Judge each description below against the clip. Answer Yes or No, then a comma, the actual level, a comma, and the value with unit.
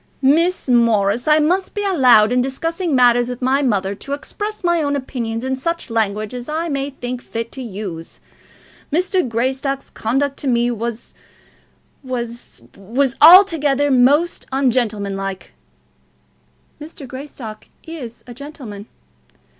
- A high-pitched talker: Yes, very high, 255 Hz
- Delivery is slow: Yes, slow, 130 wpm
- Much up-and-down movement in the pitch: No, average, 4.1 semitones